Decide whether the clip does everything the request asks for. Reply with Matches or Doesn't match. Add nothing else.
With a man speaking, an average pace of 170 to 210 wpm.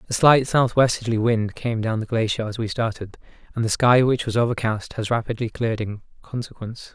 Matches